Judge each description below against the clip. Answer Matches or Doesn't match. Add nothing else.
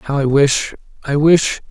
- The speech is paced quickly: Doesn't match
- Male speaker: Matches